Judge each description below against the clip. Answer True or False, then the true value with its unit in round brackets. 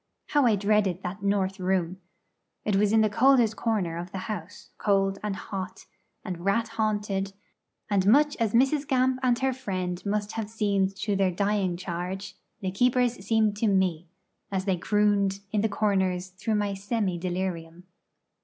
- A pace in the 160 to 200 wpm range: True (165 wpm)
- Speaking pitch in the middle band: False (200 Hz)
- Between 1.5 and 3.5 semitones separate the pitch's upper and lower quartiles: True (2.5 semitones)